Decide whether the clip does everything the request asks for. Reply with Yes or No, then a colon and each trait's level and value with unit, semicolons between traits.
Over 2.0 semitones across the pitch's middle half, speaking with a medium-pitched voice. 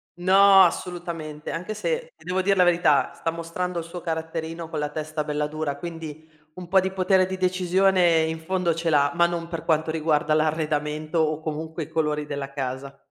Yes: average, 2.7 semitones; medium, 165 Hz